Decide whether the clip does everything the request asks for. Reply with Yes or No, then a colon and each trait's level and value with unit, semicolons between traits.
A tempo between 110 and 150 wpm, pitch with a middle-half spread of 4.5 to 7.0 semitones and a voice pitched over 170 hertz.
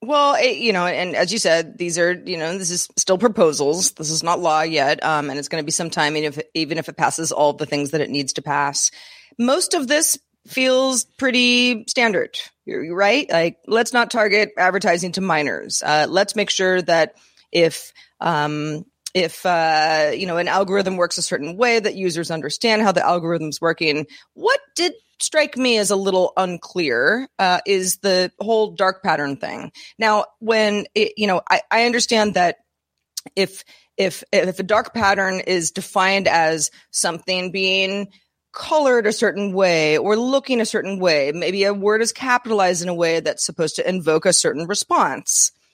No: average, 185 wpm; average, 4.9 semitones; high, 190 Hz